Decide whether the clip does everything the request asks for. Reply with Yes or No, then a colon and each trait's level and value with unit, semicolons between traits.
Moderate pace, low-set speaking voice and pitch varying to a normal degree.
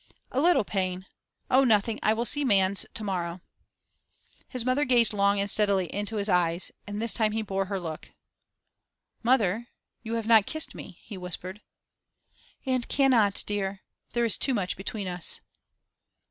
No: average, 160 wpm; high, 210 Hz; average, 3.5 semitones